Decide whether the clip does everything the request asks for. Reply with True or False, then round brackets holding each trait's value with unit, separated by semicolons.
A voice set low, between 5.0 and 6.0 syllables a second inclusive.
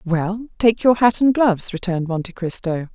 False (200 Hz; 5.1 syllables/s)